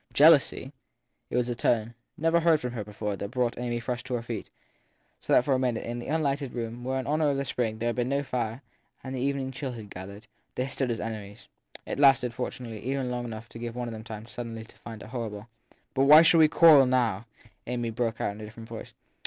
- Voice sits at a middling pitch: No, low, 120 Hz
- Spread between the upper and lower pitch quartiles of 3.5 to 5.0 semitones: No, average, 2.9 semitones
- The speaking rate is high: Yes, fast, 245 wpm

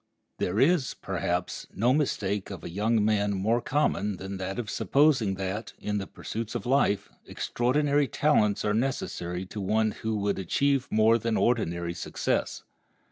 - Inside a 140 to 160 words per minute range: Yes, average, 155 wpm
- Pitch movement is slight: No, average, 3.9 semitones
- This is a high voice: No, low, 105 Hz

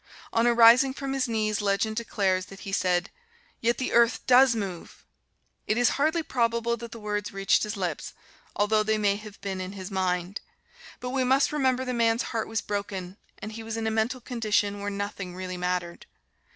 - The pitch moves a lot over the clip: No, average, 3.2 semitones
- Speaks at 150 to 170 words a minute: No, average, 190 wpm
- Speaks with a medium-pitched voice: No, high, 215 Hz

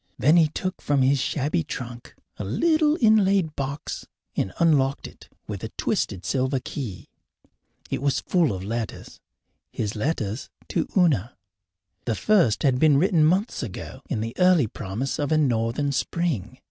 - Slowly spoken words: No, average, 155 wpm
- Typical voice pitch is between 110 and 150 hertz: Yes, medium, 140 Hz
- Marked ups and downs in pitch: Yes, wide, 6.2 semitones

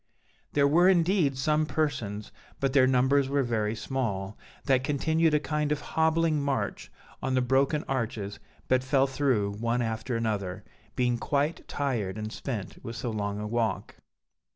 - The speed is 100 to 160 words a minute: Yes, average, 155 wpm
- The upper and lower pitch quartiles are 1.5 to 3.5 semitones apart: No, average, 4.5 semitones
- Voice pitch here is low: Yes, low, 130 Hz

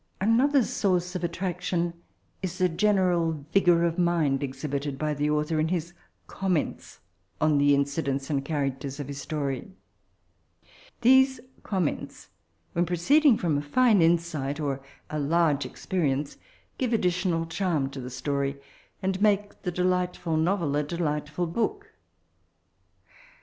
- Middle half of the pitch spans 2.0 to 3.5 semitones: No, average, 4.2 semitones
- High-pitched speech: No, medium, 165 Hz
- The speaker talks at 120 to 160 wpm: Yes, slow, 135 wpm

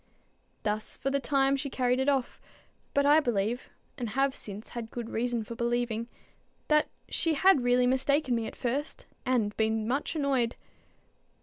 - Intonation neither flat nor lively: Yes, average, 3.2 semitones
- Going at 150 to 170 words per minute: Yes, average, 165 wpm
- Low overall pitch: No, high, 245 Hz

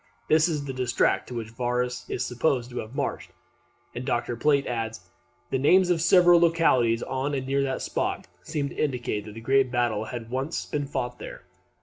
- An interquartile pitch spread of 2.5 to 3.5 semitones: Yes, average, 3.1 semitones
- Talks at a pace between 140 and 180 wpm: No, average, 200 wpm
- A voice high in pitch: No, low, 130 Hz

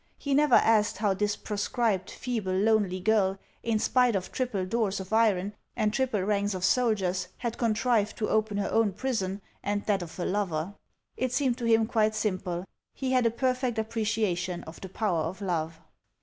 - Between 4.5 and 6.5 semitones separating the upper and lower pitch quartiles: No, average, 3.3 semitones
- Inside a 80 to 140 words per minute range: No, average, 180 wpm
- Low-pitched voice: No, high, 210 Hz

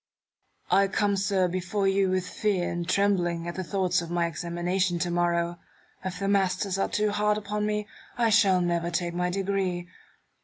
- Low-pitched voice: No, medium, 185 Hz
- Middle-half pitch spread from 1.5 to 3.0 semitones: Yes, narrow, 2.4 semitones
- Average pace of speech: Yes, average, 180 wpm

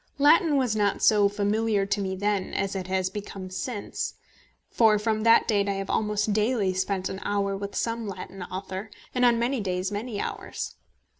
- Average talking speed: Yes, average, 180 wpm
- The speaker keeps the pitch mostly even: Yes, narrow, 2.3 semitones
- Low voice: No, high, 205 Hz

